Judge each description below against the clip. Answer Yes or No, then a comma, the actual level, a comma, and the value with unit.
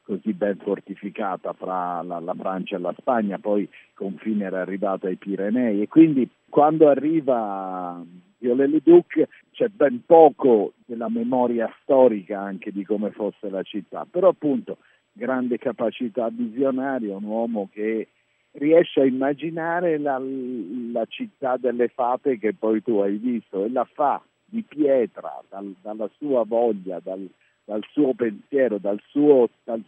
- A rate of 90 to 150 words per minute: Yes, average, 145 wpm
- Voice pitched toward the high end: No, low, 115 Hz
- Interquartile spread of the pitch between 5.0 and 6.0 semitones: Yes, wide, 5.4 semitones